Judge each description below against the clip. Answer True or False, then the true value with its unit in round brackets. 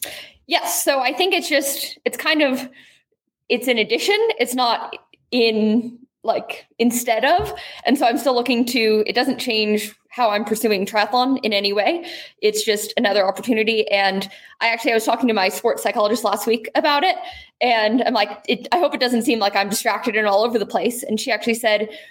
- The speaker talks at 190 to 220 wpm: True (200 wpm)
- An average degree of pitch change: True (3.6 semitones)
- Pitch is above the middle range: True (230 Hz)